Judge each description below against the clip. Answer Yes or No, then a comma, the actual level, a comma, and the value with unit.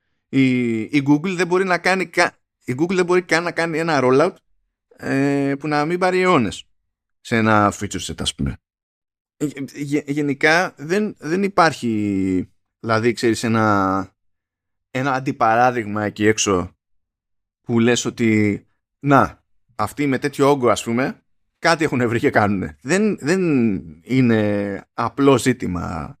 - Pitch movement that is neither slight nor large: No, wide, 6.5 semitones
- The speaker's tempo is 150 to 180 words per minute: No, average, 140 wpm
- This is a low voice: Yes, low, 120 Hz